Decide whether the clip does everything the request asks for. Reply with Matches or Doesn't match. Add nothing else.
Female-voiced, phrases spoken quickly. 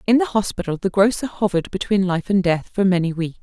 Matches